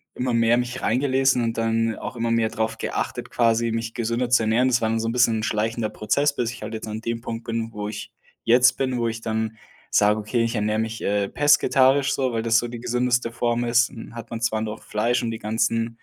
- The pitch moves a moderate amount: No, narrow, 1.5 semitones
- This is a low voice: Yes, low, 115 Hz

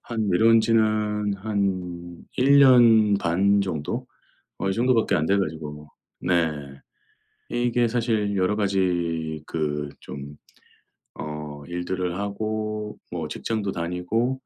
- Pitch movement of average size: Yes, average, 4.4 semitones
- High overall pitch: No, low, 100 Hz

